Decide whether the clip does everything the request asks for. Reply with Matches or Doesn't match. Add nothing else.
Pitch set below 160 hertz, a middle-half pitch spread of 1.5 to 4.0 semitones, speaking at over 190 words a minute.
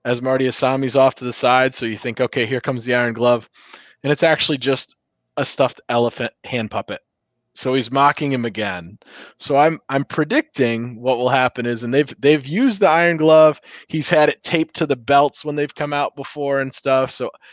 Matches